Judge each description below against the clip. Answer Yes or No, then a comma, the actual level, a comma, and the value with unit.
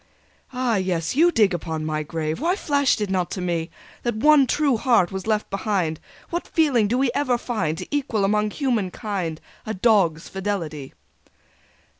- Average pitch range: No, wide, 6.3 semitones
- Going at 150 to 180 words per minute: Yes, average, 170 wpm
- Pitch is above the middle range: Yes, high, 210 Hz